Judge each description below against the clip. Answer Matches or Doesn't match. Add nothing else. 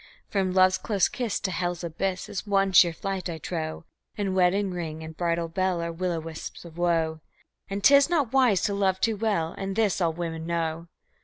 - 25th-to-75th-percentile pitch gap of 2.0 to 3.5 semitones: Matches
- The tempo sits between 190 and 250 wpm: Matches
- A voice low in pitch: Doesn't match